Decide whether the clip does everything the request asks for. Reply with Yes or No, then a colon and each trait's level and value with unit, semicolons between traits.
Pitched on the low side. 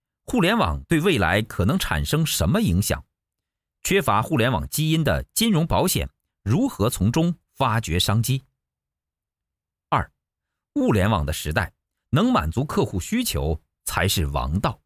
Yes: low, 100 Hz